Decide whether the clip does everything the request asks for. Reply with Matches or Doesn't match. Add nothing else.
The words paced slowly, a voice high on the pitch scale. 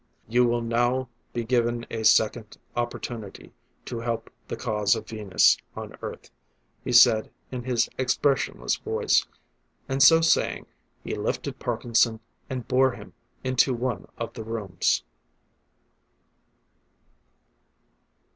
Doesn't match